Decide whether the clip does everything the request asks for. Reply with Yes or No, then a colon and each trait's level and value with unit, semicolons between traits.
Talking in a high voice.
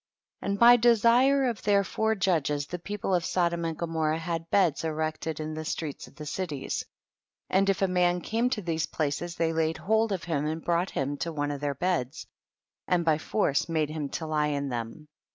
No: medium, 165 Hz